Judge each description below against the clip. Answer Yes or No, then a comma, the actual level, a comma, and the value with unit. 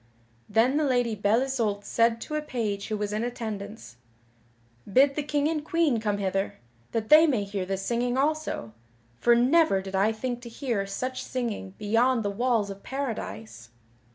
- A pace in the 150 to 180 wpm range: Yes, average, 175 wpm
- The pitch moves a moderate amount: Yes, average, 4.4 semitones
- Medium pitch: No, high, 230 Hz